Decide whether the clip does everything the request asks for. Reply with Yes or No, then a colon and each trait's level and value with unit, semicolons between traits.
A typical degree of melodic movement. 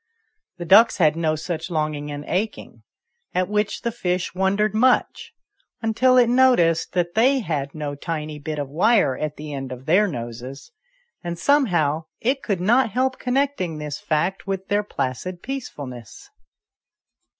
No: wide, 6.7 semitones